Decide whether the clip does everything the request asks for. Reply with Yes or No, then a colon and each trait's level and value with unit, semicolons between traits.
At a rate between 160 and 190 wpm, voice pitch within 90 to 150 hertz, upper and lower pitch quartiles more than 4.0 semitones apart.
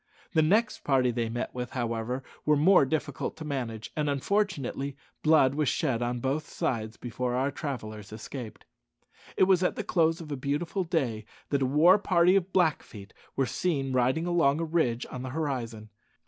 Yes: average, 175 wpm; medium, 140 Hz; average, 4.8 semitones